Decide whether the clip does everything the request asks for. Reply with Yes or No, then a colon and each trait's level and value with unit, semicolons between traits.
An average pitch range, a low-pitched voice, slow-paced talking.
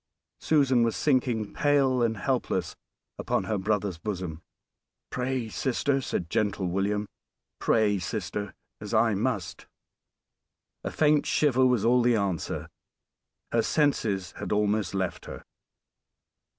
Yes: average, 4.5 semitones; low, 110 Hz; slow, 120 wpm